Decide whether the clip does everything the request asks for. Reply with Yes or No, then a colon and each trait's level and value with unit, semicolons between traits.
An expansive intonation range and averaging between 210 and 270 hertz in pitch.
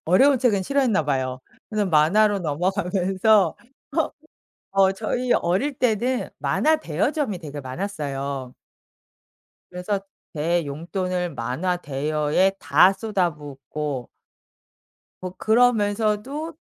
No: wide, 6.0 semitones; medium, 185 Hz